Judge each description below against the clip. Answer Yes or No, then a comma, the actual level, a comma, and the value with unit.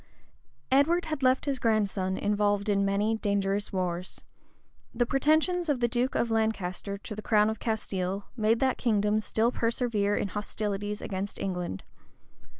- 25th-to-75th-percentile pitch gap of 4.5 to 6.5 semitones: No, average, 3.1 semitones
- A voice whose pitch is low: No, high, 215 Hz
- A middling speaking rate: Yes, average, 150 wpm